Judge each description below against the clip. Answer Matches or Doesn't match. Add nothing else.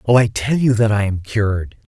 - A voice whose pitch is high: Doesn't match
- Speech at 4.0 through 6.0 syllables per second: Matches